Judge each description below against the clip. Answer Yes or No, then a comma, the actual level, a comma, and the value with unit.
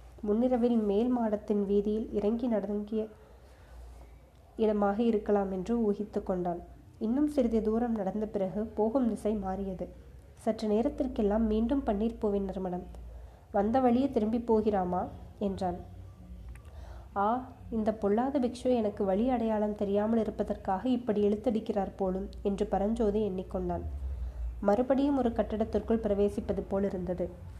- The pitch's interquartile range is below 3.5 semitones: Yes, average, 2.8 semitones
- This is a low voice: No, high, 210 Hz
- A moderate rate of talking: Yes, average, 110 wpm